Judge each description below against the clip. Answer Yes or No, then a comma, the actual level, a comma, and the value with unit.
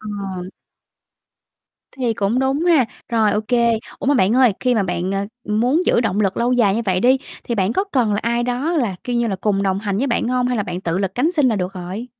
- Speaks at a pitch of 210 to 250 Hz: Yes, high, 225 Hz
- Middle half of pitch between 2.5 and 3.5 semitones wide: No, average, 4.2 semitones